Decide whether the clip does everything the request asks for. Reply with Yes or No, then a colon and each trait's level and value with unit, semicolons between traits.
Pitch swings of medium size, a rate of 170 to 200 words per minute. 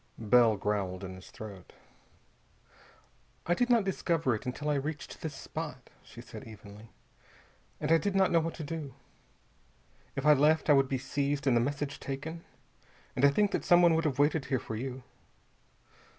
Yes: average, 4.8 semitones; average, 180 wpm